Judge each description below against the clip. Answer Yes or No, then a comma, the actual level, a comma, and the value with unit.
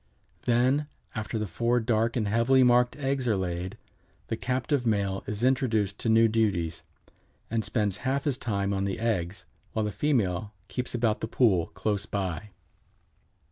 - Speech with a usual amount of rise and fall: Yes, average, 3.6 semitones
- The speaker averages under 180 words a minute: Yes, average, 160 wpm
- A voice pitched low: Yes, low, 110 Hz